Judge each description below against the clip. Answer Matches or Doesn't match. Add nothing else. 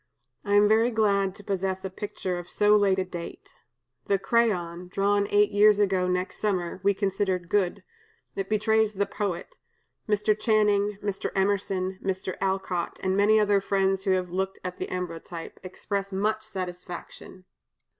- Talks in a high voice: Matches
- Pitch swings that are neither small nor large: Doesn't match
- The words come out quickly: Doesn't match